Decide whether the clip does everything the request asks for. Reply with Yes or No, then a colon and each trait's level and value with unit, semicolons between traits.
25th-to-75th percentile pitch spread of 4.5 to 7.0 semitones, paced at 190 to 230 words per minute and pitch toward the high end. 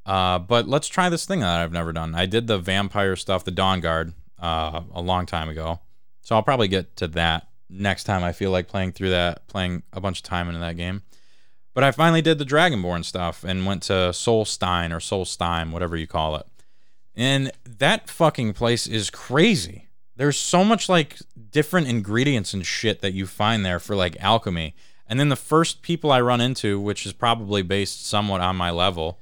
No: average, 5.2 semitones; fast, 205 wpm; low, 100 Hz